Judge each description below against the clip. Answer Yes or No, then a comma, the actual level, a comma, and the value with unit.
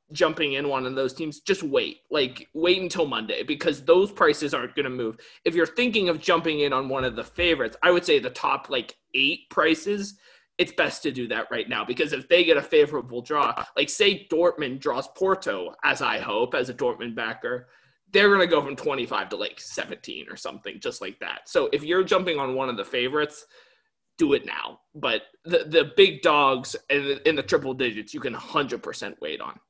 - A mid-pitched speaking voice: Yes, medium, 180 Hz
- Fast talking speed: Yes, fast, 215 wpm